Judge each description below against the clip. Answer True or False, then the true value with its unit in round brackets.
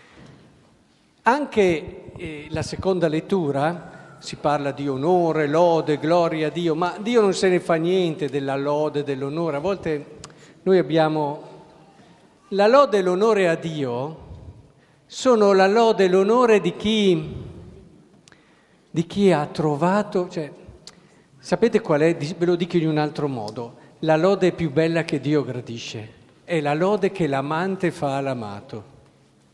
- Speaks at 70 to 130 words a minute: False (140 wpm)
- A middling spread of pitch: True (4.0 semitones)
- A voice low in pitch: False (160 Hz)